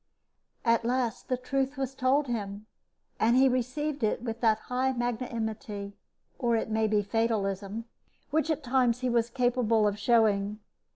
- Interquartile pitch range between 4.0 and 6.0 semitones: No, average, 2.8 semitones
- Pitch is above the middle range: Yes, high, 235 Hz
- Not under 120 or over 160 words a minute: Yes, average, 155 wpm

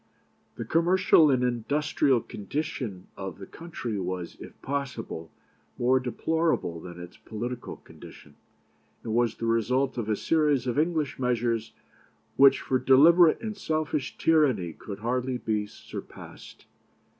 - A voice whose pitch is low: Yes, low, 125 Hz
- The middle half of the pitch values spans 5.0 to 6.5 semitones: Yes, wide, 5.4 semitones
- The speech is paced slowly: Yes, slow, 130 wpm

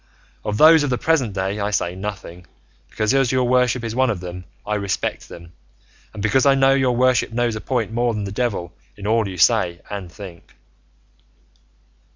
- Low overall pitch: Yes, low, 110 Hz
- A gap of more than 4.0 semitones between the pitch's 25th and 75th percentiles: Yes, average, 4.5 semitones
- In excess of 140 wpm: Yes, average, 190 wpm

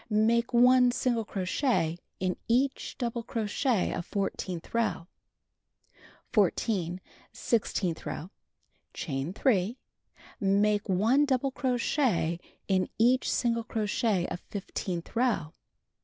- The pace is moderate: No, slow, 100 wpm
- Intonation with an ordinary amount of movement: Yes, average, 4.8 semitones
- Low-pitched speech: No, high, 215 Hz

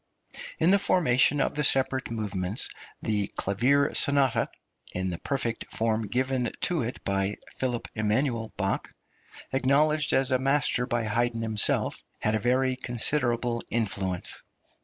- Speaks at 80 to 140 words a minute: Yes, slow, 135 wpm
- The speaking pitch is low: Yes, low, 120 Hz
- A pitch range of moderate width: Yes, average, 3.7 semitones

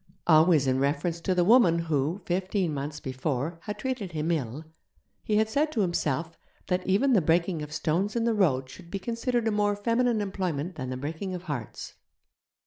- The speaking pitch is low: No, medium, 175 Hz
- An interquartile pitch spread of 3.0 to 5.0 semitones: No, wide, 5.4 semitones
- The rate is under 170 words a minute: No, average, 190 wpm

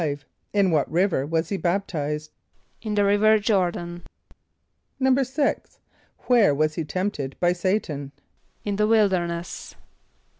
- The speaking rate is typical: No, slow, 120 wpm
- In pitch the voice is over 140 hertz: Yes, medium, 185 Hz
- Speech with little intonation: No, average, 4.6 semitones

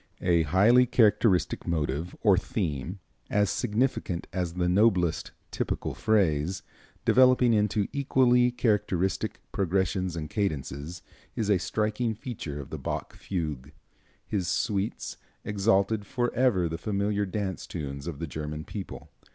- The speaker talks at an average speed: No, slow, 125 wpm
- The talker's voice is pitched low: Yes, very low, 95 Hz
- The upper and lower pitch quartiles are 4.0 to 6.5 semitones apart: Yes, average, 4.5 semitones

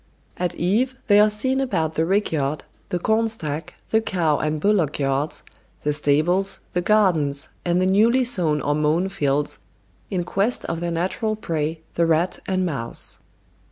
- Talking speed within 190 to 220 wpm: No, average, 165 wpm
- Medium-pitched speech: Yes, medium, 175 Hz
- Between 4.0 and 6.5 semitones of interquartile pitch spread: Yes, average, 5.1 semitones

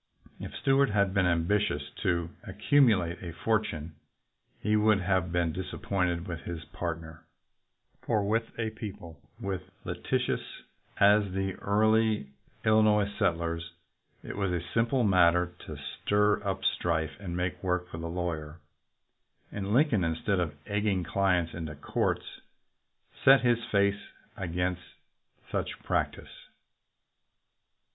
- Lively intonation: No, average, 3.6 semitones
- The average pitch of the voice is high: No, very low, 95 Hz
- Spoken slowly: Yes, slow, 125 wpm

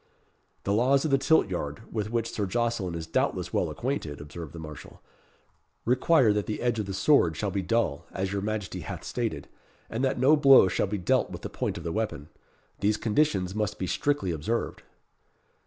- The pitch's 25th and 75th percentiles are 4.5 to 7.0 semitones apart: Yes, average, 5.1 semitones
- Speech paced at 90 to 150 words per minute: No, average, 195 wpm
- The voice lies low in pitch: Yes, low, 105 Hz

